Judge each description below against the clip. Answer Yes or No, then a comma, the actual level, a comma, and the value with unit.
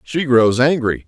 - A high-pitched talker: No, low, 130 Hz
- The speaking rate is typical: Yes, average, 165 wpm